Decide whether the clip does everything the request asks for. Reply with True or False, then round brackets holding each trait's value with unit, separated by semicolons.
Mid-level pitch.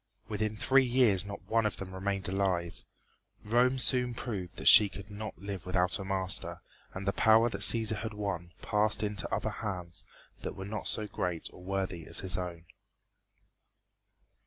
False (100 Hz)